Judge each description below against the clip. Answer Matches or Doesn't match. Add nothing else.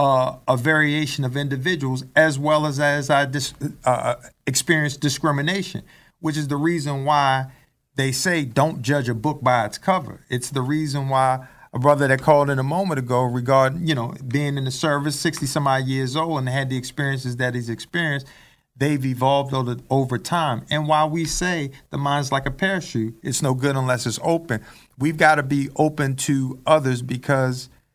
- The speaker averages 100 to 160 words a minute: Doesn't match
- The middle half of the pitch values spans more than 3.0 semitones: Doesn't match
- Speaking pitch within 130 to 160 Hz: Matches